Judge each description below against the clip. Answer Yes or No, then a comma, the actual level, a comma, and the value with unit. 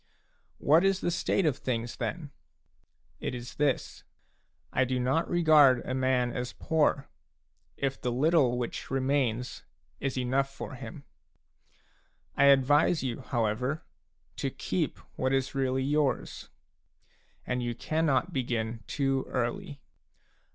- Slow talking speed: Yes, slow, 125 wpm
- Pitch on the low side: Yes, low, 130 Hz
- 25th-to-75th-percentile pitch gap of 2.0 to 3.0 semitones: Yes, average, 2.7 semitones